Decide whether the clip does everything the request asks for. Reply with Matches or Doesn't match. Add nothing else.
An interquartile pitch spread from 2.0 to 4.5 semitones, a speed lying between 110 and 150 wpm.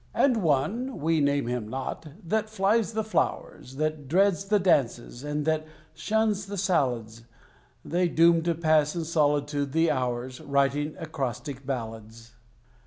Doesn't match